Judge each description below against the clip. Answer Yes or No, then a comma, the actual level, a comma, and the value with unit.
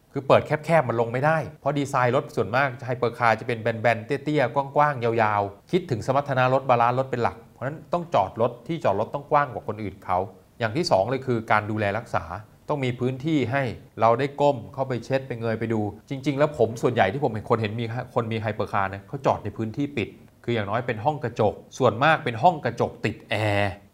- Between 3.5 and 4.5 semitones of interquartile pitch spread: Yes, average, 4.1 semitones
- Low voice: Yes, low, 120 Hz